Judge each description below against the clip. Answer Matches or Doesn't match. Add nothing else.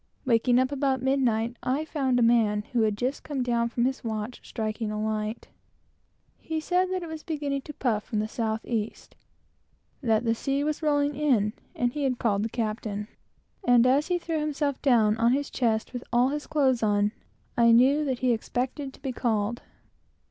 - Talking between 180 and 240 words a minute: Matches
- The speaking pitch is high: Matches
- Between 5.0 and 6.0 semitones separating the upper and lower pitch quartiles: Doesn't match